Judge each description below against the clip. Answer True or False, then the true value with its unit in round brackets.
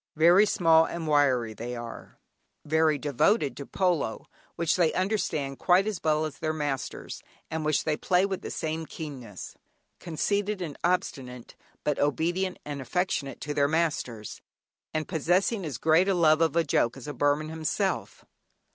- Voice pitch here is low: False (155 Hz)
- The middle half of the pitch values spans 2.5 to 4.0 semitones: True (3.6 semitones)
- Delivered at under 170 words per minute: True (160 wpm)